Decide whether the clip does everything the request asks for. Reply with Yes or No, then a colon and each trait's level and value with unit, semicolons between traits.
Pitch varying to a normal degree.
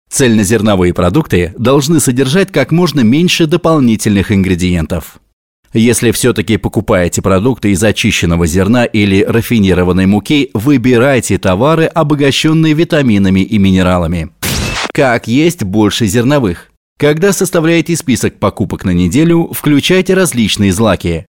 No: wide, 7.4 semitones